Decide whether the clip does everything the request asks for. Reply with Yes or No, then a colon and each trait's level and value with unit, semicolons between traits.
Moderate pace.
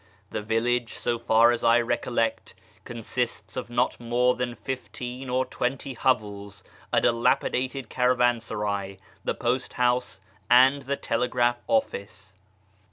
No: slow, 125 wpm